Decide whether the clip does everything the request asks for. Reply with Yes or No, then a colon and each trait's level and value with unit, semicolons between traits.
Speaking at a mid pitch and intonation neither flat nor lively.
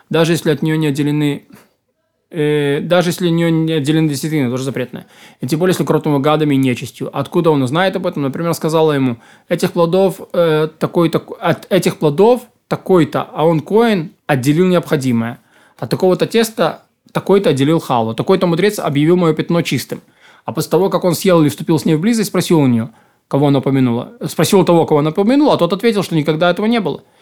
Yes: medium, 160 Hz; average, 3.3 semitones